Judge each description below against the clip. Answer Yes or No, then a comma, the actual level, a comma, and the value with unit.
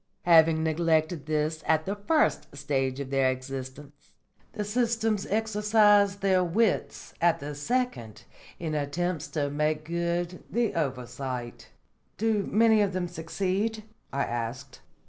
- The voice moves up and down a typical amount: No, wide, 6.2 semitones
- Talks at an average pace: No, slow, 125 wpm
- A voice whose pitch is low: No, medium, 165 Hz